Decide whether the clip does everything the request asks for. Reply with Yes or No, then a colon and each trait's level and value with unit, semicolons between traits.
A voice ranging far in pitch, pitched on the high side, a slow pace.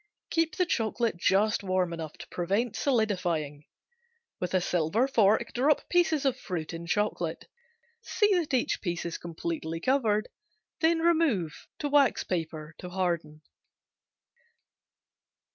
Yes: wide, 7.9 semitones; high, 200 Hz; slow, 125 wpm